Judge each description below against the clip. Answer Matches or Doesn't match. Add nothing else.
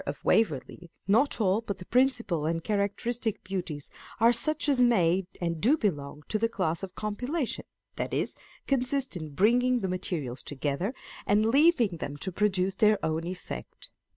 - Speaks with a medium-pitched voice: Doesn't match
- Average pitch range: Doesn't match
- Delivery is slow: Doesn't match